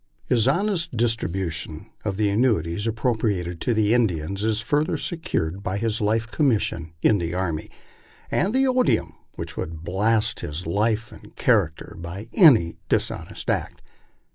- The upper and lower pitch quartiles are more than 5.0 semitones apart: Yes, wide, 5.4 semitones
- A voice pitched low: Yes, low, 105 Hz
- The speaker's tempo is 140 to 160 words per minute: Yes, average, 145 wpm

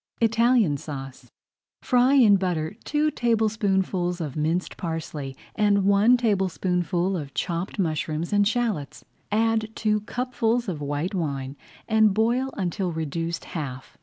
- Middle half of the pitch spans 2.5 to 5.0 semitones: No, wide, 5.5 semitones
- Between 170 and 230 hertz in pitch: Yes, high, 190 Hz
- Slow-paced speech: Yes, slow, 125 wpm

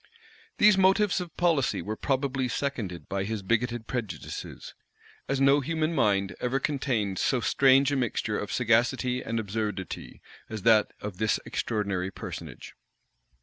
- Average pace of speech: Yes, average, 145 wpm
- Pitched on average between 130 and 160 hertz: No, low, 120 Hz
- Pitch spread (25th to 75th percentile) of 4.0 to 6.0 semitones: Yes, average, 4.8 semitones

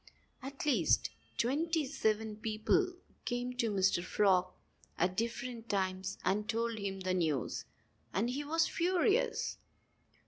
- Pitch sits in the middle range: No, high, 225 Hz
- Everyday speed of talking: No, slow, 125 wpm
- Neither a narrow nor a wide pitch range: No, wide, 6.0 semitones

